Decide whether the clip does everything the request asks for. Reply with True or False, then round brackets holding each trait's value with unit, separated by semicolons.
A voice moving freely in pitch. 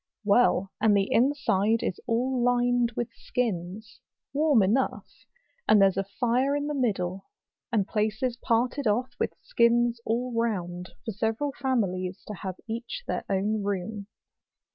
False (3.7 semitones)